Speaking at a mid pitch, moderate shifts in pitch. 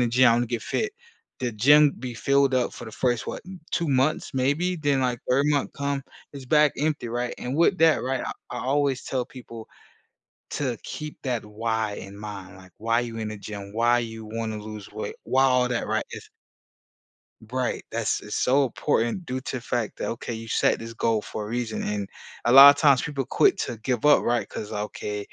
No: low, 125 Hz; average, 3.6 semitones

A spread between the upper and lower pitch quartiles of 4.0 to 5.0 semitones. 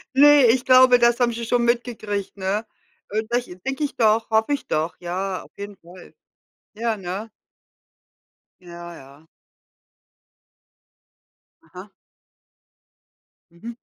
Yes: average, 4.5 semitones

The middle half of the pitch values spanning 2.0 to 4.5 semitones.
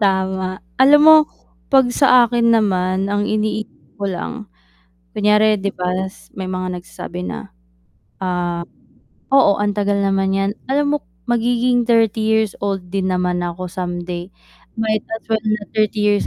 Yes: average, 3.0 semitones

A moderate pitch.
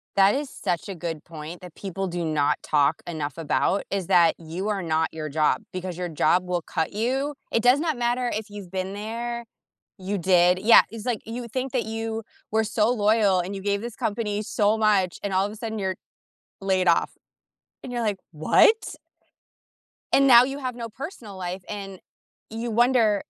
No: high, 205 Hz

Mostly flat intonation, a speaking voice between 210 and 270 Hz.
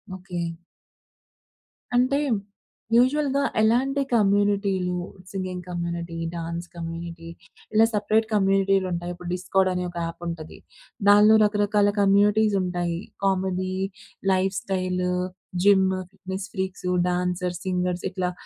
No: narrow, 2.3 semitones; medium, 185 Hz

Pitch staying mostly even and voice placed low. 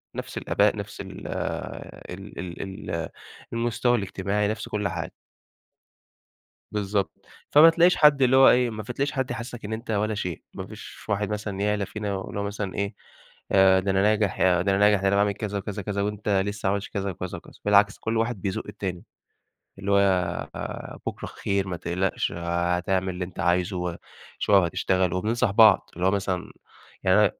Yes: narrow, 2.2 semitones; low, 100 Hz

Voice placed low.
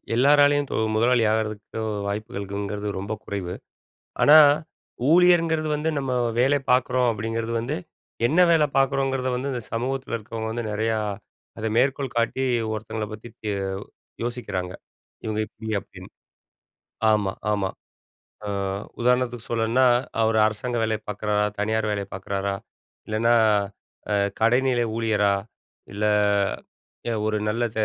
Yes: low, 115 Hz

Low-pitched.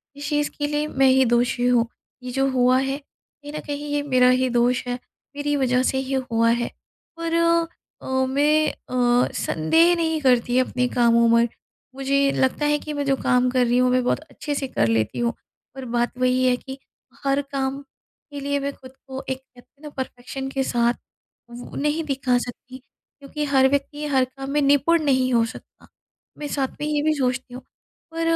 No: very high, 265 Hz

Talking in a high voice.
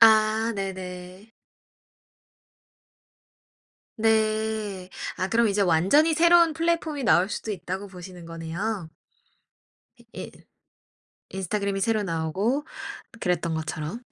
Yes: high, 200 Hz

